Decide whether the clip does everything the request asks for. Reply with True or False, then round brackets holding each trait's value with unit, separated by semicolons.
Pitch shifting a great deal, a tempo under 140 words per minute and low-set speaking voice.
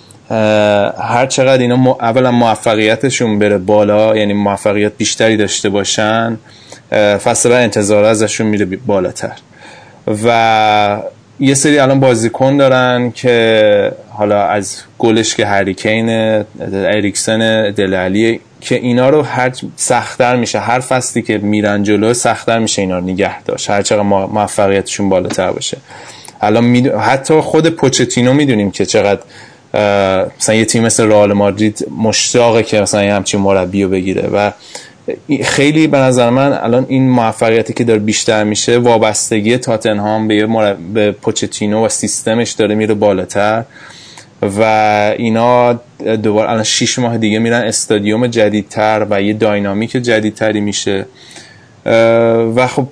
False (2.5 semitones; 130 wpm; 110 Hz)